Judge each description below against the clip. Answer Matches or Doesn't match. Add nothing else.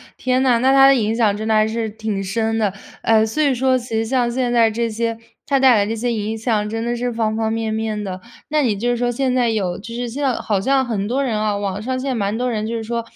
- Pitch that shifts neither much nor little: Doesn't match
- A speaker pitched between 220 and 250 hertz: Matches